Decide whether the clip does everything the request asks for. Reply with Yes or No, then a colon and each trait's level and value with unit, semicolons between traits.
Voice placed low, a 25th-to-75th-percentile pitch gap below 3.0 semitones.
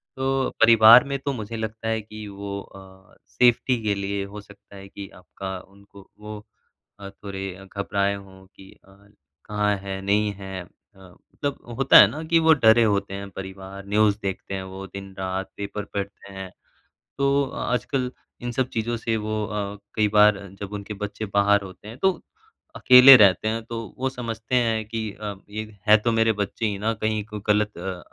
Yes: low, 105 Hz; narrow, 2.5 semitones